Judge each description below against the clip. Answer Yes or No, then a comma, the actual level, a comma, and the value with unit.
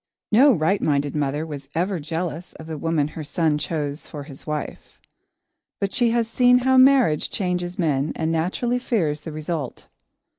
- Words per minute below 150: No, average, 165 wpm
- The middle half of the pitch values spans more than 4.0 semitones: Yes, average, 5.0 semitones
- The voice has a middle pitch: Yes, medium, 160 Hz